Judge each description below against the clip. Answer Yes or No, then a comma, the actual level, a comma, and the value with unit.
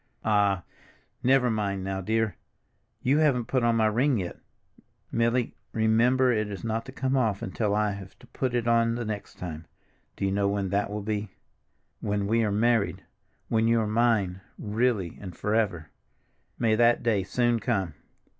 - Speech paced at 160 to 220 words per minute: Yes, average, 165 wpm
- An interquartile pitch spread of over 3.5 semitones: No, average, 2.9 semitones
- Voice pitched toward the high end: No, low, 110 Hz